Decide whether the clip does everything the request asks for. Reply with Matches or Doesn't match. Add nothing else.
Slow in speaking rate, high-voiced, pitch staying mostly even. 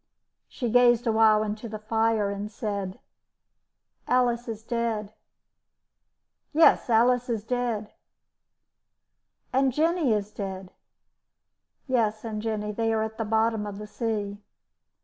Matches